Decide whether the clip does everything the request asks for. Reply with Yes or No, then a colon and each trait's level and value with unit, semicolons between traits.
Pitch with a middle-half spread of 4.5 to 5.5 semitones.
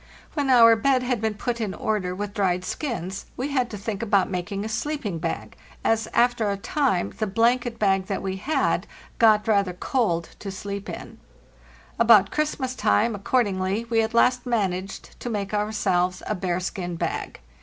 No: average, 3.6 semitones